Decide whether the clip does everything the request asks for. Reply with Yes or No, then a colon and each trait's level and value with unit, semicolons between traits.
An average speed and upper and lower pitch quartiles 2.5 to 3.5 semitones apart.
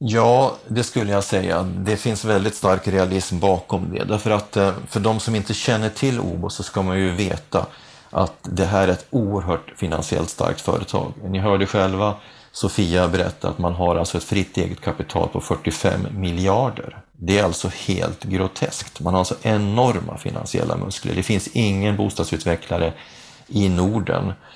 Yes: average, 165 wpm; average, 2.9 semitones